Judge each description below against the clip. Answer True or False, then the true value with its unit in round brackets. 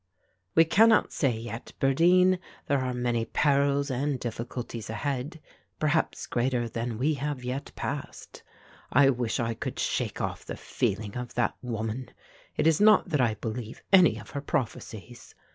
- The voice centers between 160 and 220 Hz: False (130 Hz)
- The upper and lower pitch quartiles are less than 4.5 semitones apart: True (3.9 semitones)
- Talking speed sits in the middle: True (155 wpm)